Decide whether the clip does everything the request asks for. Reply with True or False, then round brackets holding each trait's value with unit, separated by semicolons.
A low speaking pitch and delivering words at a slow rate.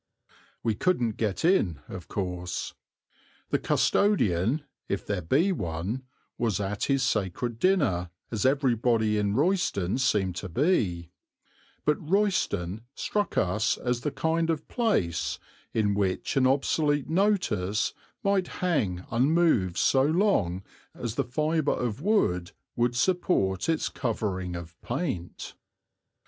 True (120 Hz; 125 wpm)